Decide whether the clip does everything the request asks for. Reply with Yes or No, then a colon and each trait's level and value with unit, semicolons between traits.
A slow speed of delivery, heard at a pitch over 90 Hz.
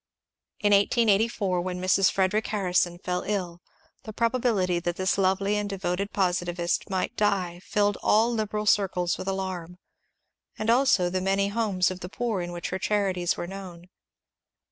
No: average, 155 wpm; high, 190 Hz